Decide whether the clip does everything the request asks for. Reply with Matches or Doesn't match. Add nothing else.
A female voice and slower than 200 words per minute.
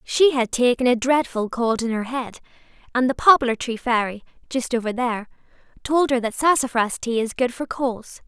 Matches